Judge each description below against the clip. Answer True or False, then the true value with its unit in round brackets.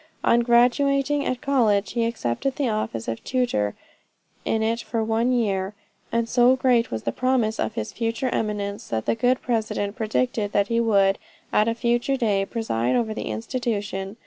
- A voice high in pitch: True (230 Hz)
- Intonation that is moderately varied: True (3.3 semitones)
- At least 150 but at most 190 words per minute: True (170 wpm)